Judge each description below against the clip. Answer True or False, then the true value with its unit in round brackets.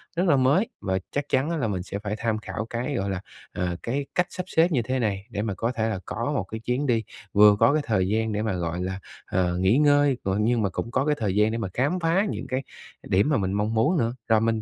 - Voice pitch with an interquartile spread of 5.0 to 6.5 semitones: True (5.4 semitones)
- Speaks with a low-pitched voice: True (115 Hz)